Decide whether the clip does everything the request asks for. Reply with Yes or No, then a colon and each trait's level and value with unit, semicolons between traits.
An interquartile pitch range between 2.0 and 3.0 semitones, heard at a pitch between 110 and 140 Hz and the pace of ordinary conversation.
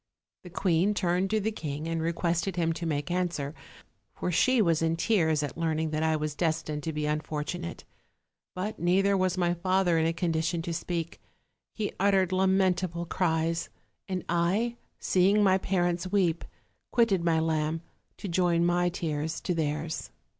No: narrow, 2.5 semitones; medium, 170 Hz; average, 165 wpm